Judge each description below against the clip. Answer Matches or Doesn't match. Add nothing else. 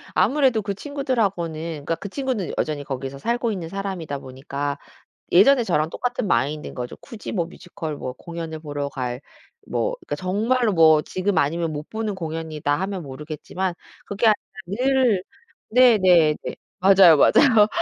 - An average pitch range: Doesn't match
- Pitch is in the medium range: Matches